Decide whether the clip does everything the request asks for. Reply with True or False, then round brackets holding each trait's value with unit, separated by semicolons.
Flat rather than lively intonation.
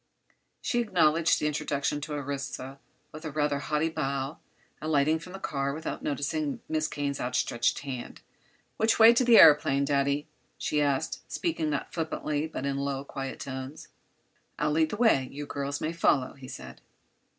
True (2.2 semitones)